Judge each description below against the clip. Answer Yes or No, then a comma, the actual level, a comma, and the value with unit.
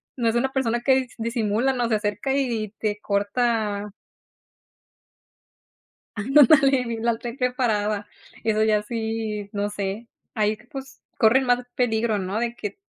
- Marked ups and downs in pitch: No, average, 2.9 semitones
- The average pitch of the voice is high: Yes, high, 225 Hz